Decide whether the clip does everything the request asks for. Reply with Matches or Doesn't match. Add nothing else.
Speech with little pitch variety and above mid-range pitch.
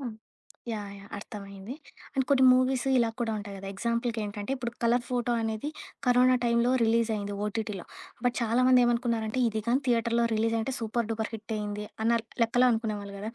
Matches